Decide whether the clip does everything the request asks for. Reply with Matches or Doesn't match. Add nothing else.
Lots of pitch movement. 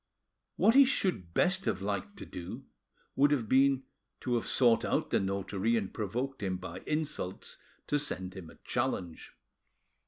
Matches